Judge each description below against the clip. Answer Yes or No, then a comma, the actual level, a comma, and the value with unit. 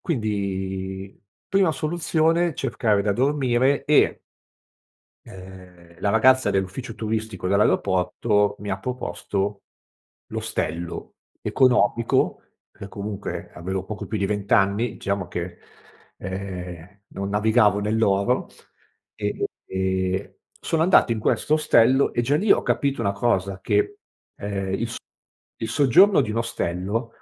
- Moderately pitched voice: No, low, 105 Hz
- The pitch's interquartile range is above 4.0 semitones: Yes, average, 4.5 semitones